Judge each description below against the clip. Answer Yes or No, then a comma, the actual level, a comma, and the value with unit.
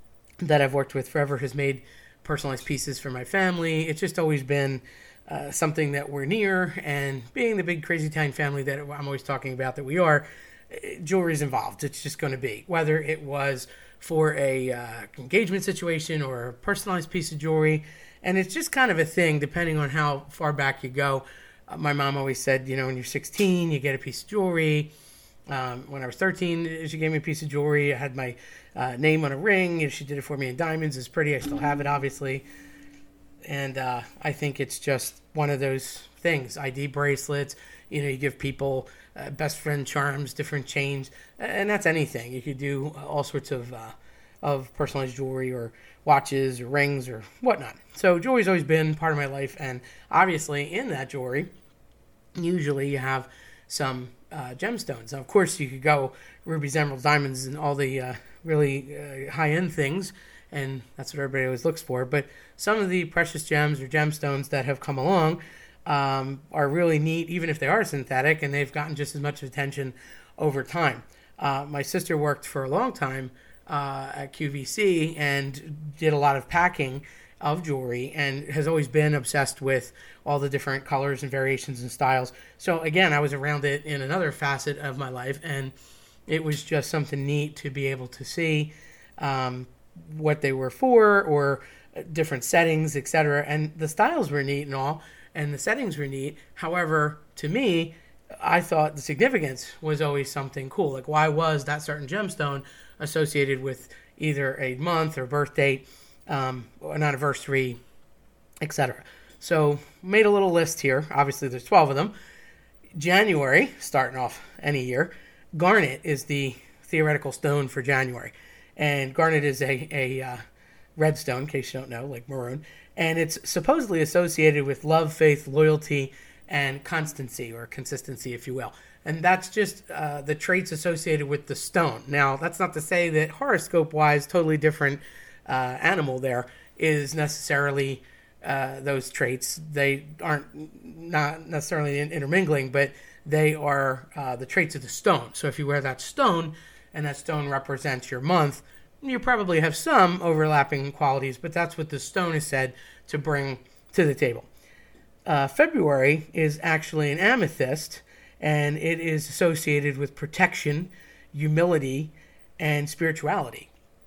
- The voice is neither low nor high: Yes, medium, 145 Hz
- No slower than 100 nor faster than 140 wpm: No, average, 175 wpm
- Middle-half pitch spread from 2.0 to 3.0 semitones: Yes, average, 2.7 semitones